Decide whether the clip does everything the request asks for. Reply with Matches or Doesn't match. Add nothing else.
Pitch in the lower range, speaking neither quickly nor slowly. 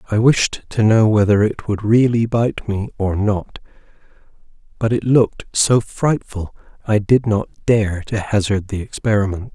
Matches